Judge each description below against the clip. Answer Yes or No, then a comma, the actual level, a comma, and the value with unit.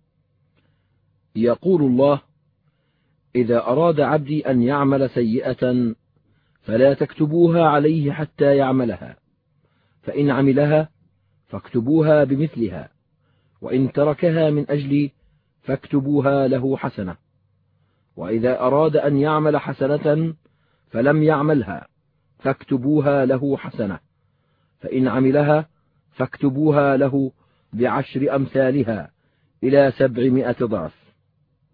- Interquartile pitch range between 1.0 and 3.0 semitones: Yes, narrow, 2.5 semitones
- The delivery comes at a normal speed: Yes, average, 80 wpm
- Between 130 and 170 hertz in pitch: Yes, medium, 140 Hz